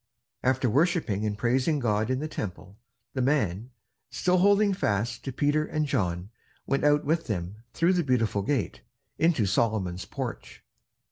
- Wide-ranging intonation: Yes, wide, 6.6 semitones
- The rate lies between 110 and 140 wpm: No, average, 150 wpm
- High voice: No, low, 125 Hz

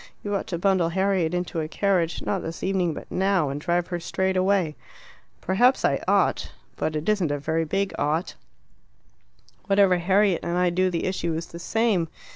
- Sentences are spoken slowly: No, average, 185 wpm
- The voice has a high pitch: No, medium, 180 Hz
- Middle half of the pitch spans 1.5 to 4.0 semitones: Yes, average, 2.8 semitones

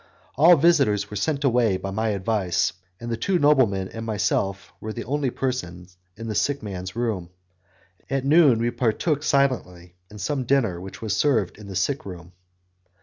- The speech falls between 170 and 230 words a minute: Yes, average, 175 wpm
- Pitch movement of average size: No, wide, 6.0 semitones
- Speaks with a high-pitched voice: No, low, 115 Hz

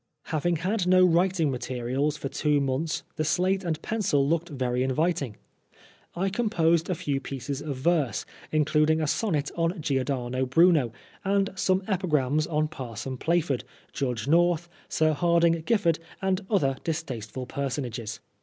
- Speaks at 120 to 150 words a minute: Yes, average, 140 wpm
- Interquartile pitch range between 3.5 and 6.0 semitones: Yes, average, 4.4 semitones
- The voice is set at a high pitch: No, medium, 155 Hz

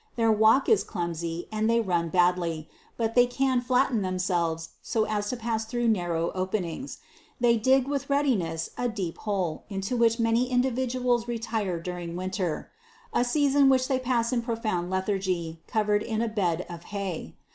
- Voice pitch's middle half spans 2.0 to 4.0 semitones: No, average, 5.3 semitones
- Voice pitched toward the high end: Yes, high, 215 Hz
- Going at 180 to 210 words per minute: No, average, 165 wpm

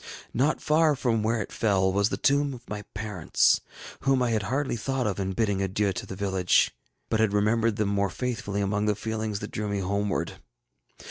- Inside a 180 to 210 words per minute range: Yes, average, 200 wpm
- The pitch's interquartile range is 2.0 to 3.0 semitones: Yes, average, 2.7 semitones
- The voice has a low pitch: Yes, low, 105 Hz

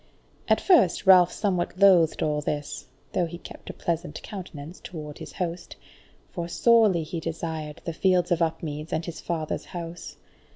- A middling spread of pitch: No, narrow, 2.3 semitones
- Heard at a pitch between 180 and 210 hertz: No, medium, 170 Hz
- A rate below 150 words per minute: No, average, 160 wpm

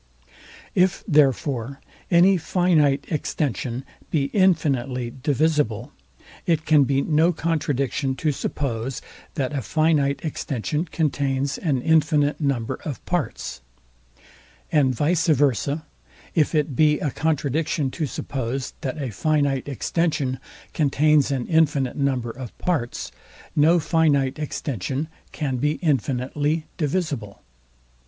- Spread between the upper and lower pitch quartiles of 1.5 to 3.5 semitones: Yes, average, 3.0 semitones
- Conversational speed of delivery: No, slow, 110 wpm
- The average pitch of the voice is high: No, medium, 145 Hz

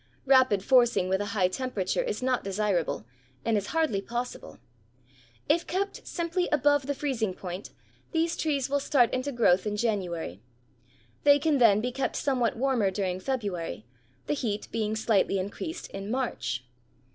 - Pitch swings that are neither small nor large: No, wide, 5.9 semitones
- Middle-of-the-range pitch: No, high, 235 Hz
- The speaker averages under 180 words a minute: Yes, average, 155 wpm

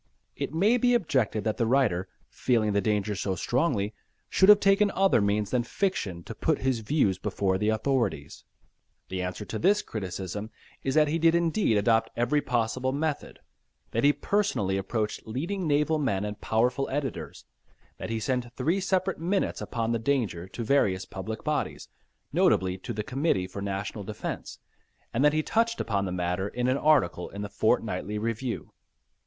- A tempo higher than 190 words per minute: No, average, 170 wpm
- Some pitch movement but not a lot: No, wide, 6.7 semitones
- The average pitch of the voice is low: Yes, low, 115 Hz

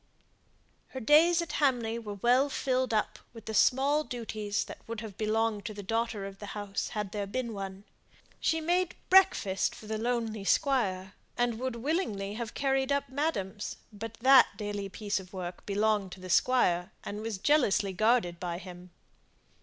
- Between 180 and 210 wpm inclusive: No, average, 170 wpm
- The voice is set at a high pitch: Yes, high, 220 Hz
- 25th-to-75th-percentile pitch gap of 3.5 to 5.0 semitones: Yes, average, 4.5 semitones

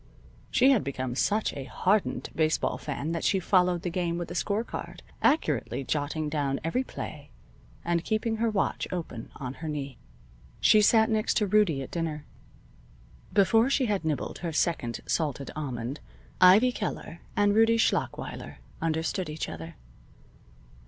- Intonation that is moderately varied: No, wide, 6.3 semitones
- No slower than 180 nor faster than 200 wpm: No, average, 150 wpm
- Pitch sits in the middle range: Yes, medium, 170 Hz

